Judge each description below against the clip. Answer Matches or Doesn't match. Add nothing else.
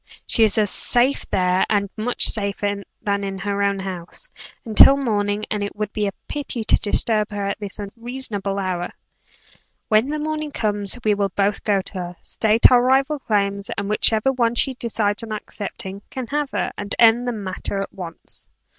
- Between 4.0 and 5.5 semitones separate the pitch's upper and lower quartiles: Doesn't match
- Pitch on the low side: Doesn't match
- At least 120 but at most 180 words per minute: Doesn't match